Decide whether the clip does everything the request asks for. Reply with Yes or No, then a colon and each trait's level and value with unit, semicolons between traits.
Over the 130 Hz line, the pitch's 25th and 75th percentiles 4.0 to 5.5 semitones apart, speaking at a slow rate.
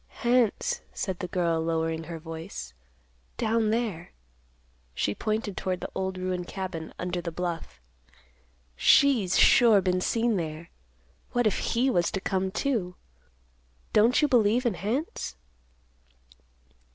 Yes: high, 190 Hz; average, 4.9 semitones; slow, 130 wpm